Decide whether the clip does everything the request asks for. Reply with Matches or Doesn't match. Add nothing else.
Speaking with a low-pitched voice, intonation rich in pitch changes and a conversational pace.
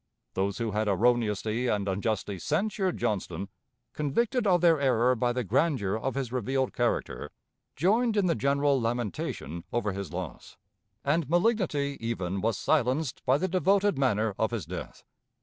Matches